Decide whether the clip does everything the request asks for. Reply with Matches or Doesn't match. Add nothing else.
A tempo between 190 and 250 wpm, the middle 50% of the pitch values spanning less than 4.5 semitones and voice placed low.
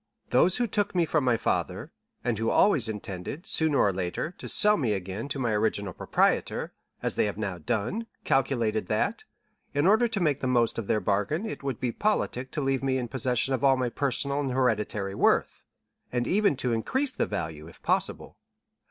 Doesn't match